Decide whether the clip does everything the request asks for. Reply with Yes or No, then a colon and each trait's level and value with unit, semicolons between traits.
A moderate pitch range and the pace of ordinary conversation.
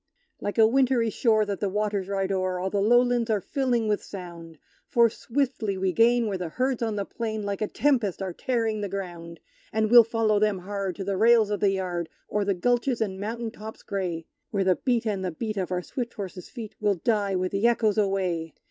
No: average, 3.3 semitones; fast, 220 wpm